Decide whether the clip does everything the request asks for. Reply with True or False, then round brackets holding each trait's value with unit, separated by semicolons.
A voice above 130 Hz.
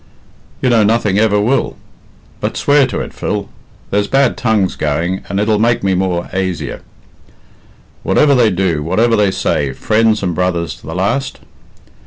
False (100 Hz)